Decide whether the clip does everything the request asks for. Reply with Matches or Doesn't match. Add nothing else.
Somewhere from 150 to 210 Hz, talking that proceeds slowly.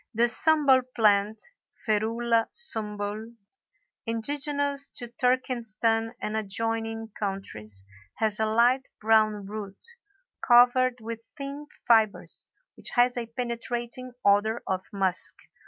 Doesn't match